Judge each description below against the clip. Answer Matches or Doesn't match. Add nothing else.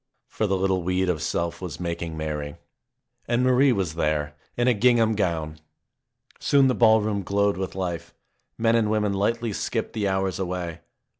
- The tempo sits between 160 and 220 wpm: Matches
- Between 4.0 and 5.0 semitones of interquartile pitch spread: Matches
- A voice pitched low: Matches